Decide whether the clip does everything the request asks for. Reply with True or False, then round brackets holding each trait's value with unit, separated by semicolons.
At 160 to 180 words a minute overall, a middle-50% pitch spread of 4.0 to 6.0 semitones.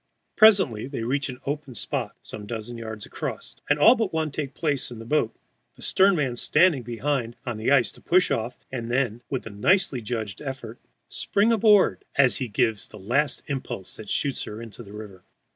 False (195 wpm; 4.8 semitones)